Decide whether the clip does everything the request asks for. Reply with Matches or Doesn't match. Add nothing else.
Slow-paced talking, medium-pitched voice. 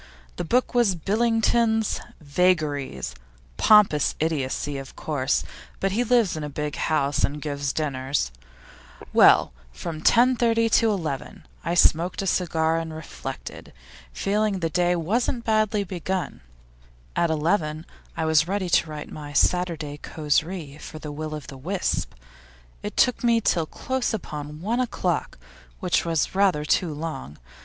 Doesn't match